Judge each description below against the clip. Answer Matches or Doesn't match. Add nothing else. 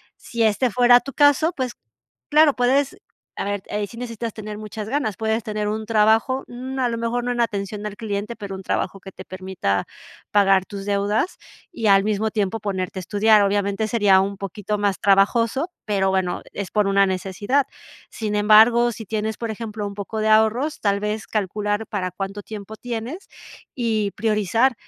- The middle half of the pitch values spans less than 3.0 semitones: Matches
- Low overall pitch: Doesn't match